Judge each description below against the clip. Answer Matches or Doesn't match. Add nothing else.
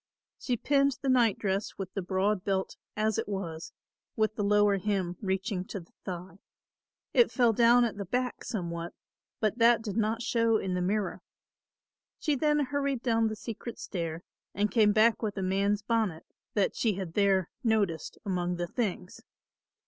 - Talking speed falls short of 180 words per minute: Matches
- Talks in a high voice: Matches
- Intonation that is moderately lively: Matches